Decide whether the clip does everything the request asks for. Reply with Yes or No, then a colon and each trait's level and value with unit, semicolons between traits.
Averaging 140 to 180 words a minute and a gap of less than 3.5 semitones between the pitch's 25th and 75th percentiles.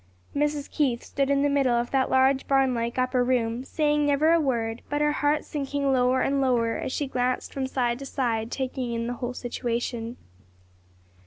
No: average, 190 wpm; average, 2.7 semitones